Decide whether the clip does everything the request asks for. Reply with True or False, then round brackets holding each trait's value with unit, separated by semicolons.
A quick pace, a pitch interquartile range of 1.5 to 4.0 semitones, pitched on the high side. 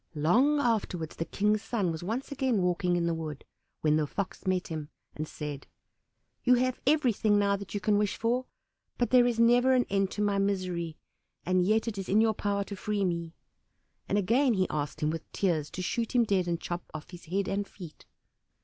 False (210 wpm; 4.8 semitones; 200 Hz)